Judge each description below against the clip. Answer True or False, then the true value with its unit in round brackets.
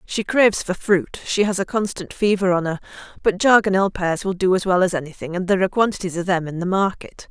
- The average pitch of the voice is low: False (190 Hz)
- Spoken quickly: True (230 wpm)